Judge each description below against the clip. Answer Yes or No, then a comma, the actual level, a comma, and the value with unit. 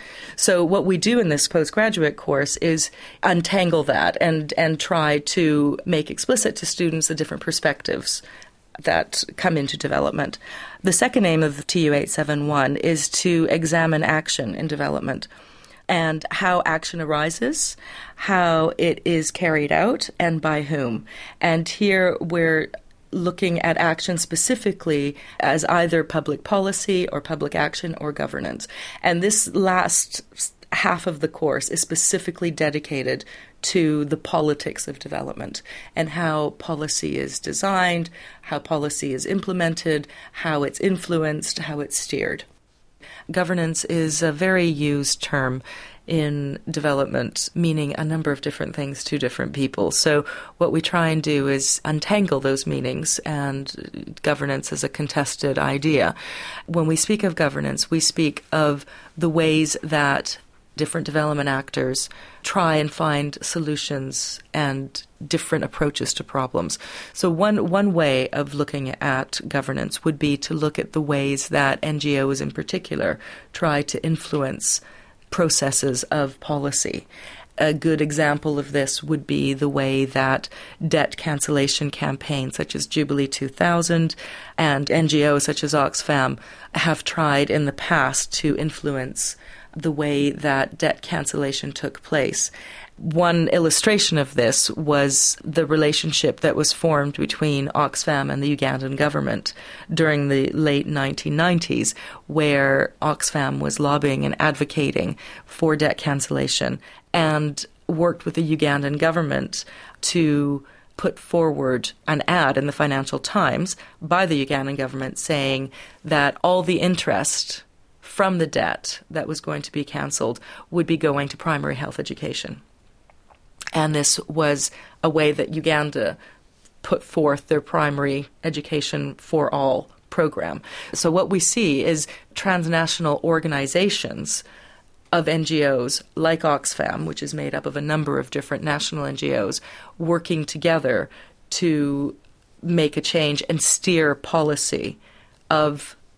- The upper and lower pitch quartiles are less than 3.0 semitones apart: Yes, narrow, 2.5 semitones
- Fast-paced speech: No, slow, 135 wpm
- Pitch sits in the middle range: Yes, medium, 155 Hz